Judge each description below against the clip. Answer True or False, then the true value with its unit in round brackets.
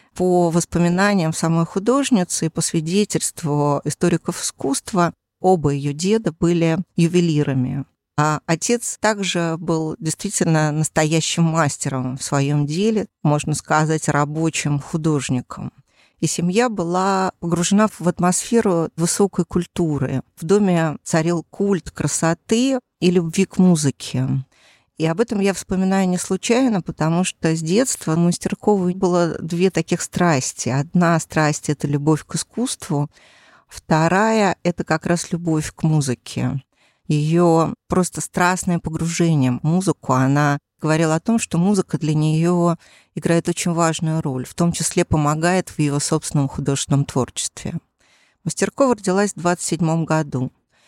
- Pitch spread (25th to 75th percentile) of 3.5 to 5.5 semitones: False (3.1 semitones)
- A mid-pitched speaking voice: True (165 Hz)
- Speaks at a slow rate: False (125 wpm)